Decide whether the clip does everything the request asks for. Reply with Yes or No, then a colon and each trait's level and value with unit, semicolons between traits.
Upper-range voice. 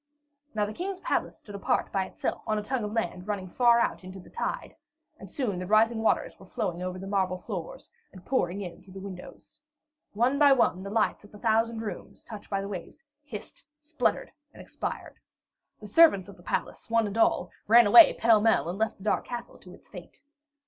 Yes: high, 210 Hz